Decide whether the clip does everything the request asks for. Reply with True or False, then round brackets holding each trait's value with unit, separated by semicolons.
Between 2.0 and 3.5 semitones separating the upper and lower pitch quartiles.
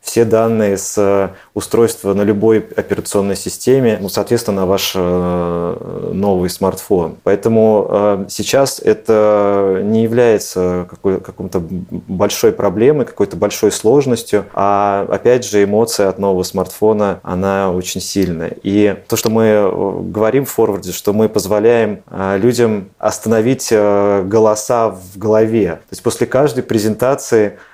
True (2.5 semitones)